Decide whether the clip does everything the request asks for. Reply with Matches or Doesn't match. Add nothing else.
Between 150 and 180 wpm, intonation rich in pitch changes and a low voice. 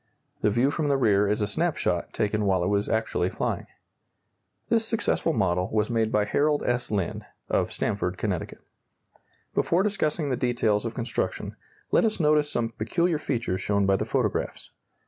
Matches